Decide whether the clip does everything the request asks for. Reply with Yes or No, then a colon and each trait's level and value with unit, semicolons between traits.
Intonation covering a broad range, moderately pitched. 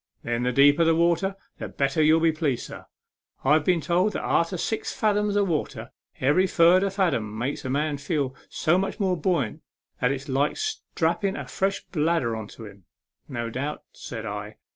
Yes: wide, 5.9 semitones; medium, 155 Hz